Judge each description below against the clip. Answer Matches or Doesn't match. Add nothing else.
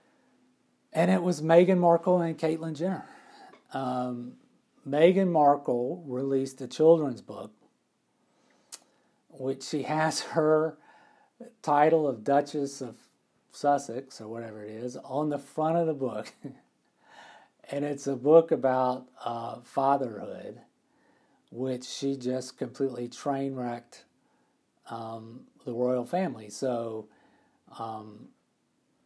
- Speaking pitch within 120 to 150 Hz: Matches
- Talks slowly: Matches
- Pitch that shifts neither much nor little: Matches